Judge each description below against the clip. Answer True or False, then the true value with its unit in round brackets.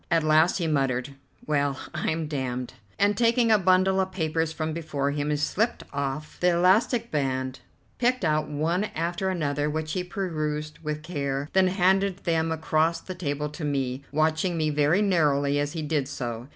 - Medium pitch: True (155 Hz)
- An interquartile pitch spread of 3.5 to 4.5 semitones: True (3.9 semitones)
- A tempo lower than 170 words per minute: False (175 wpm)